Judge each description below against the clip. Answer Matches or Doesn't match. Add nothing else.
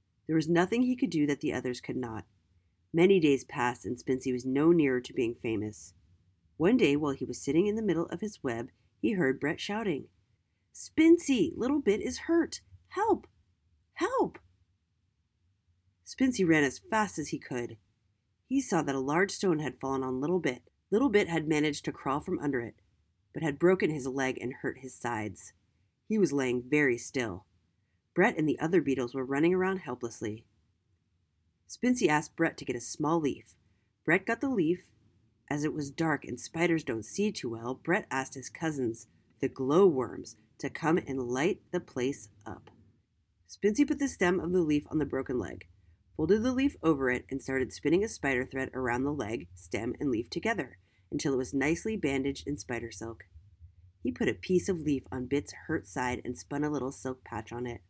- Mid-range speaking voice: Doesn't match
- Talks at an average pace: Matches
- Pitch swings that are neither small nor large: Doesn't match